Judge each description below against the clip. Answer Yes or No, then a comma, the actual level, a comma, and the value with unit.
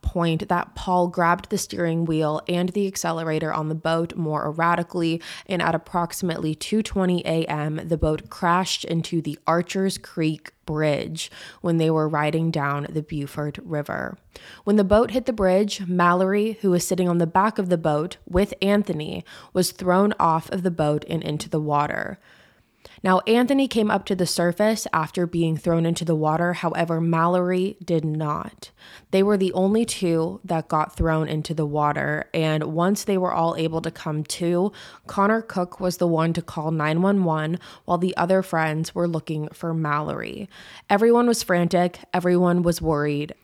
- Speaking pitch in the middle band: Yes, medium, 170 Hz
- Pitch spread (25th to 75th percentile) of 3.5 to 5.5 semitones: No, average, 2.8 semitones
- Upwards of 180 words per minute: No, average, 170 wpm